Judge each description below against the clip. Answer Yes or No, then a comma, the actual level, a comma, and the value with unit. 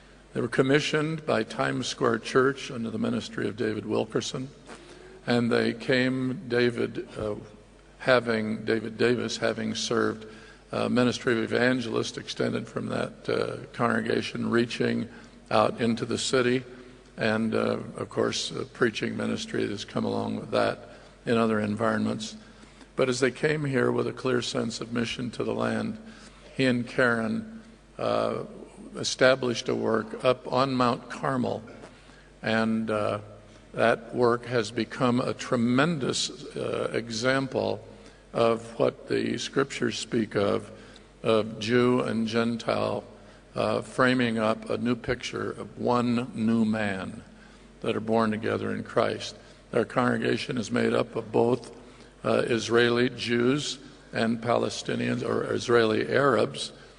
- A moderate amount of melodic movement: No, narrow, 2.1 semitones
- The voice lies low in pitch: Yes, low, 120 Hz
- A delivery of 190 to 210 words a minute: No, slow, 135 wpm